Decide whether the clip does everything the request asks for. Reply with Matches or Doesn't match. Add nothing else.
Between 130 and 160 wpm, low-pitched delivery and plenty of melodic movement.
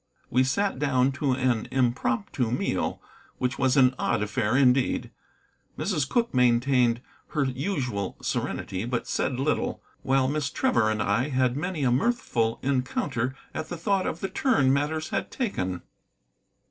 Doesn't match